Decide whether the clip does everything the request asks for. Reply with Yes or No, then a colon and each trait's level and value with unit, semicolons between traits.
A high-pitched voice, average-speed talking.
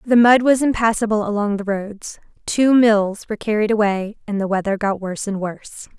Yes: high, 210 Hz; average, 190 wpm